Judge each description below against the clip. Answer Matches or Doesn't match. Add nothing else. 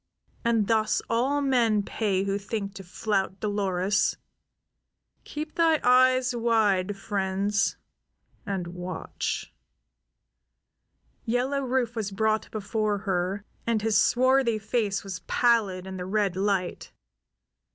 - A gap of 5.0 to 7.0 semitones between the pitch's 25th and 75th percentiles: Doesn't match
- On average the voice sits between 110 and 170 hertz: Doesn't match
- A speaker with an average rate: Doesn't match